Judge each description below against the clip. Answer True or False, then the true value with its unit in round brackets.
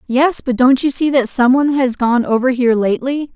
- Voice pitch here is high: True (255 Hz)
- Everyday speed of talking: False (235 wpm)